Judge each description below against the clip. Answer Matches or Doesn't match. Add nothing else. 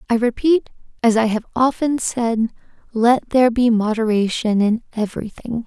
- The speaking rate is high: Doesn't match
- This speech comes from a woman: Matches